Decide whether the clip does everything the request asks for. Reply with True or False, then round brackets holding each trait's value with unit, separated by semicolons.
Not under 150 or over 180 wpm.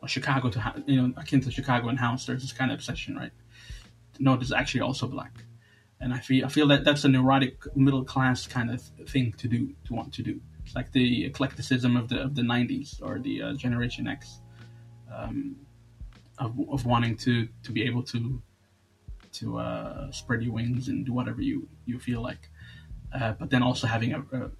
False (200 wpm)